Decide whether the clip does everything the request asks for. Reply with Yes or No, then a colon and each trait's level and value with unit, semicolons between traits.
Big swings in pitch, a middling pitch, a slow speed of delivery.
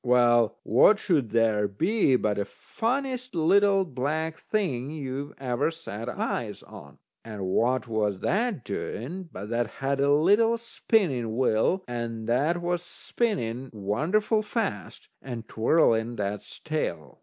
No: wide, 7.9 semitones; low, 130 Hz; slow, 130 wpm